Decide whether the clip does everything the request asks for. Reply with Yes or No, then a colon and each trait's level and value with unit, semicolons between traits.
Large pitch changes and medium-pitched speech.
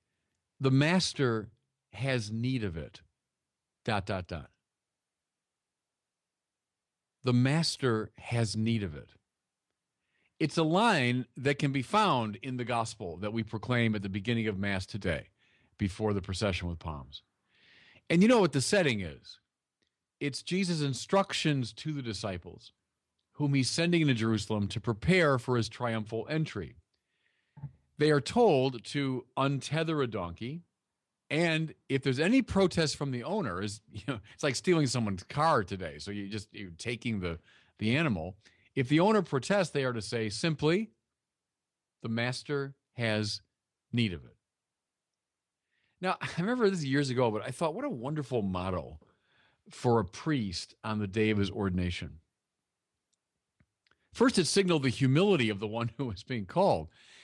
No: wide, 6.0 semitones; low, 120 Hz